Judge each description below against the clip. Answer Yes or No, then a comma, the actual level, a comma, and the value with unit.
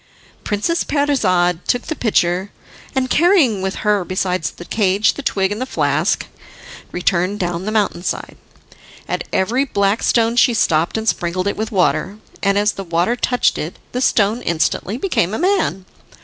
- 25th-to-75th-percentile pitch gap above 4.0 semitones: Yes, average, 4.9 semitones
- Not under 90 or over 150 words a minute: No, average, 165 wpm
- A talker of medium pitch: No, high, 205 Hz